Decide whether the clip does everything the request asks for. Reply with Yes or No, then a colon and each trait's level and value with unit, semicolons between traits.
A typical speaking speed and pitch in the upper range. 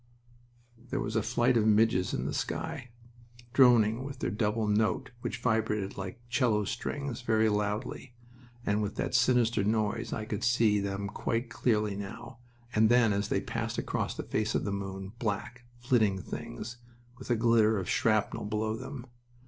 No: average, 165 wpm; low, 110 Hz